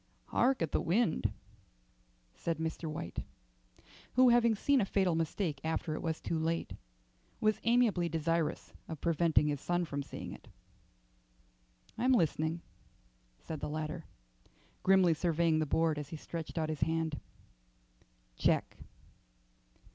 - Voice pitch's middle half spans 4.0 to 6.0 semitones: No, average, 3.0 semitones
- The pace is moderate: No, slow, 130 wpm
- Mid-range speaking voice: Yes, medium, 165 Hz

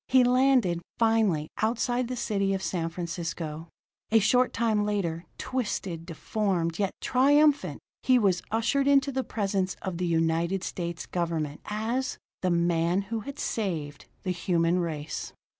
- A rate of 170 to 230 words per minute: No, average, 140 wpm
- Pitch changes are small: No, wide, 5.6 semitones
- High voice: Yes, high, 195 Hz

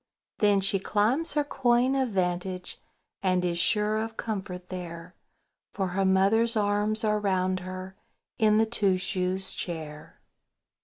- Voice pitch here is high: Yes, high, 195 Hz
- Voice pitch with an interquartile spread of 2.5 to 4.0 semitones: Yes, average, 2.9 semitones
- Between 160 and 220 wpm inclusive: No, average, 140 wpm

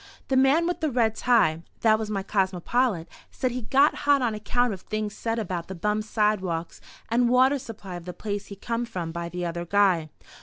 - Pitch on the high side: Yes, high, 215 Hz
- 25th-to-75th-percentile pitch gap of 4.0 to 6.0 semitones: Yes, average, 5.1 semitones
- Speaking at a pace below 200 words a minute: No, fast, 205 wpm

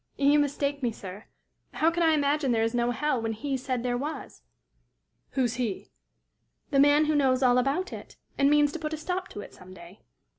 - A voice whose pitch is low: No, very high, 275 Hz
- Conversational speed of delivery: No, fast, 210 wpm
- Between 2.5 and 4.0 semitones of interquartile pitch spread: Yes, average, 3.6 semitones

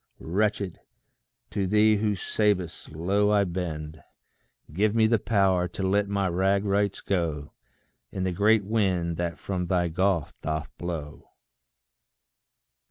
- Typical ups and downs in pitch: Yes, average, 3.0 semitones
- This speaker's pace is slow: Yes, slow, 130 wpm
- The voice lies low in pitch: Yes, very low, 95 Hz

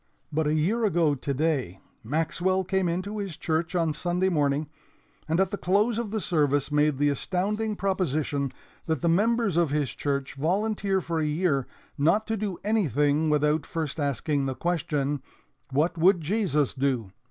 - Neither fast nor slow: Yes, average, 165 wpm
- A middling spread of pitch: Yes, average, 4.6 semitones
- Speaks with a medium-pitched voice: Yes, medium, 160 Hz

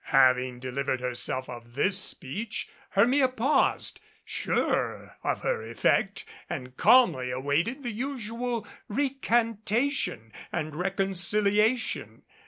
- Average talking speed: No, slow, 95 wpm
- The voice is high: Yes, high, 200 Hz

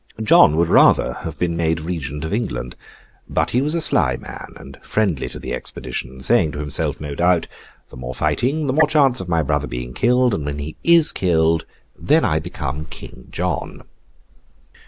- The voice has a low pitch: Yes, very low, 80 Hz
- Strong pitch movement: Yes, wide, 8.6 semitones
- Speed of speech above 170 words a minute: Yes, average, 185 wpm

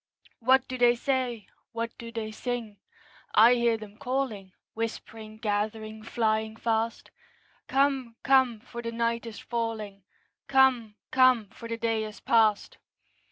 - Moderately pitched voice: No, high, 230 Hz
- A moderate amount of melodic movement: No, narrow, 2.0 semitones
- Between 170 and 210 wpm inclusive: No, slow, 135 wpm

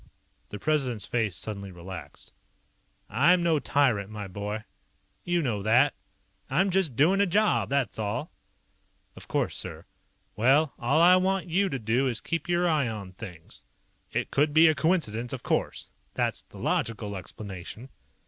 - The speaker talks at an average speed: Yes, average, 160 wpm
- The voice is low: Yes, low, 130 Hz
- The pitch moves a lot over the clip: Yes, wide, 7.7 semitones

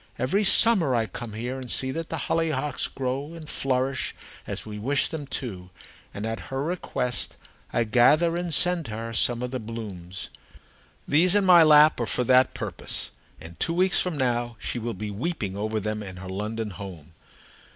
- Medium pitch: No, low, 125 Hz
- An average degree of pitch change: No, wide, 6.1 semitones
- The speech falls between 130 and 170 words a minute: No, average, 185 wpm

